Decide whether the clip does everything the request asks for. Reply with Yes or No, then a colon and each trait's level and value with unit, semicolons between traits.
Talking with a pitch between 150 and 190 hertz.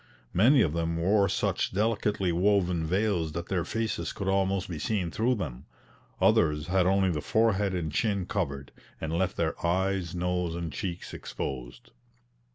No: very low, 90 Hz